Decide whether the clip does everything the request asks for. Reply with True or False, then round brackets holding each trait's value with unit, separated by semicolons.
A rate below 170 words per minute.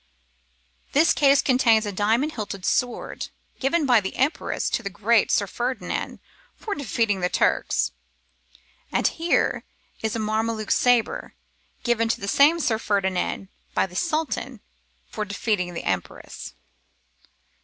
True (135 wpm)